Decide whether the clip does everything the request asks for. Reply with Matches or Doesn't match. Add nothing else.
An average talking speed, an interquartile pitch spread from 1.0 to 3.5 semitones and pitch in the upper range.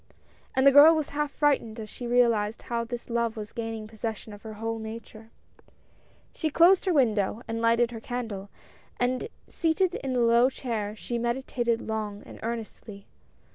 Matches